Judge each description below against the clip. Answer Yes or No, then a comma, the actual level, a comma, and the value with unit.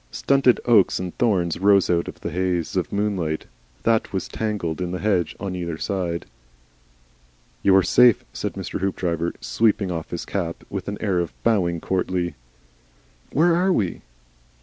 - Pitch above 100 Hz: No, very low, 95 Hz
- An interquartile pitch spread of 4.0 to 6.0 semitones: No, average, 3.4 semitones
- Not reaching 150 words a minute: No, average, 160 wpm